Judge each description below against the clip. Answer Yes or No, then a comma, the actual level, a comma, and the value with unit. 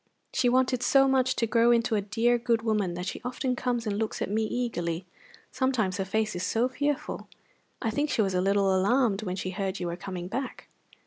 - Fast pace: Yes, fast, 215 wpm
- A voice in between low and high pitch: No, high, 220 Hz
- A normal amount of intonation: Yes, average, 4.4 semitones